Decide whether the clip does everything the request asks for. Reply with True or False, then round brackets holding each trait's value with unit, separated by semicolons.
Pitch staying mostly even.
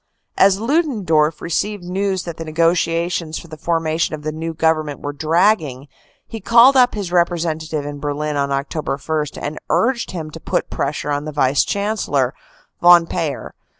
False (3.3 semitones)